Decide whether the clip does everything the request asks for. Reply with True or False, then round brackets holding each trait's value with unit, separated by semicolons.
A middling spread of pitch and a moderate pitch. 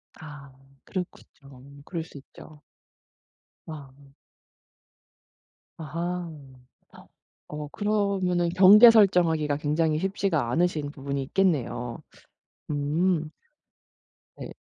True (4.0 semitones; 160 Hz)